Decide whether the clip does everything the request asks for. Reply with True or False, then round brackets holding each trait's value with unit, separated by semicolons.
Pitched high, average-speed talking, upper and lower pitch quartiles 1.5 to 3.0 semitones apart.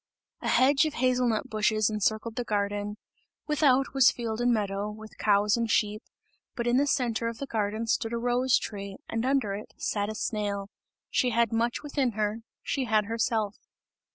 True (225 Hz; 180 wpm; 2.7 semitones)